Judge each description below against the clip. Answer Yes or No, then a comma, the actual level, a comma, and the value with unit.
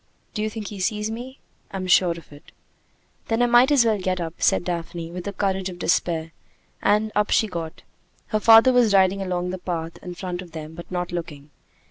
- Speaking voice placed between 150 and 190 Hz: Yes, medium, 185 Hz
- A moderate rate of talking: No, fast, 210 wpm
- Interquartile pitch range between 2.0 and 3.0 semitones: No, average, 3.7 semitones